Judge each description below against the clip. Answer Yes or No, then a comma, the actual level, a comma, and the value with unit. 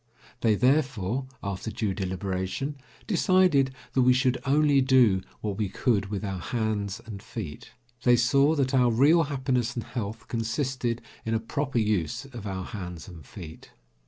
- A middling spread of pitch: Yes, average, 4.8 semitones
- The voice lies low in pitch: Yes, low, 115 Hz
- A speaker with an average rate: Yes, average, 160 wpm